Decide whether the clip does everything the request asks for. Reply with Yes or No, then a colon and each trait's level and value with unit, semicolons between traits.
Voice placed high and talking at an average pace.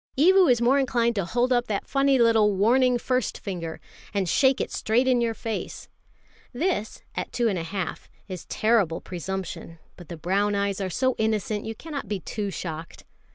Yes: high, 220 Hz; average, 185 wpm